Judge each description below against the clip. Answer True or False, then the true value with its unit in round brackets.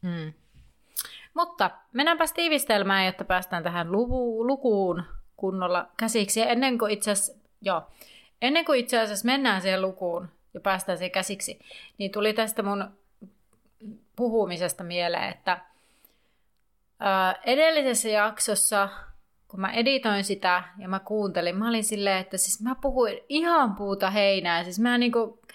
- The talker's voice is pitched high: True (210 Hz)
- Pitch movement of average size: True (3.8 semitones)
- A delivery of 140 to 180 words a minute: False (130 wpm)